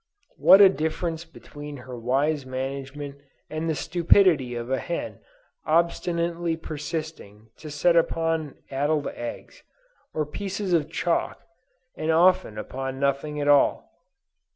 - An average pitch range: Yes, average, 3.5 semitones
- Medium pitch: Yes, medium, 155 Hz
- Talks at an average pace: No, slow, 125 wpm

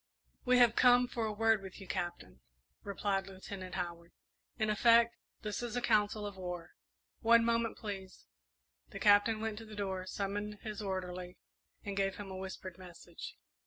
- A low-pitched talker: No, high, 205 Hz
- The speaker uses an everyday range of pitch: Yes, average, 3.0 semitones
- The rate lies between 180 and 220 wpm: No, average, 165 wpm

